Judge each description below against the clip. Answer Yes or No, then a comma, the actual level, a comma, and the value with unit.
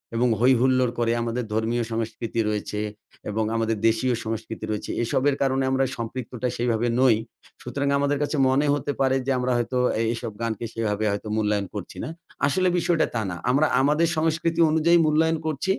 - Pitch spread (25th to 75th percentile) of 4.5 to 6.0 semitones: No, average, 4.1 semitones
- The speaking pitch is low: Yes, low, 125 Hz